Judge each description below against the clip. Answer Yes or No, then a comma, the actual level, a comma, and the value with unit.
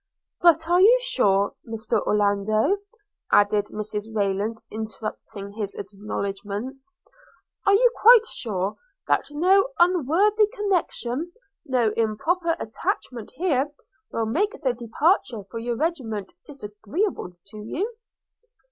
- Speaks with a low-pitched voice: No, high, 240 Hz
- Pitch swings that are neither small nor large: No, wide, 9.0 semitones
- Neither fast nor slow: No, slow, 110 wpm